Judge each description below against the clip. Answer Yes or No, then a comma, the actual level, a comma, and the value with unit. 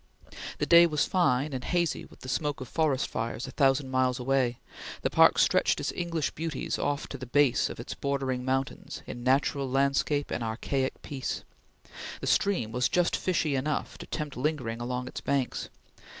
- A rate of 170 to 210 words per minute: Yes, average, 180 wpm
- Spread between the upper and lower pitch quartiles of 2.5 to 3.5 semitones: Yes, average, 2.9 semitones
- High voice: No, low, 135 Hz